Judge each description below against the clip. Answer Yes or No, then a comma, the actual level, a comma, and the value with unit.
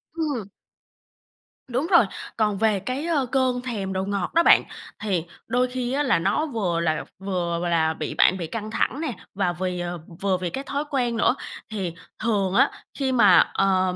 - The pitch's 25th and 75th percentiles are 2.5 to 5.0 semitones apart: No, wide, 5.6 semitones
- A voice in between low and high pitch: No, high, 205 Hz